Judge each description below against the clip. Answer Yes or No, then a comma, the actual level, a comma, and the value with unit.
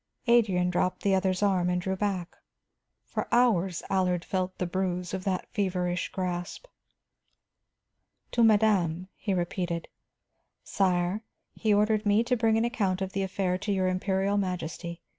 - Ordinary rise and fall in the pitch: No, narrow, 2.2 semitones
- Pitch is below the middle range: No, high, 190 Hz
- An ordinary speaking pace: Yes, average, 145 wpm